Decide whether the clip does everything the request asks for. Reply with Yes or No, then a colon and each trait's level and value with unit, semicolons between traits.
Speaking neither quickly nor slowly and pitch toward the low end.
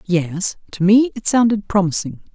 No: average, 155 wpm; high, 200 Hz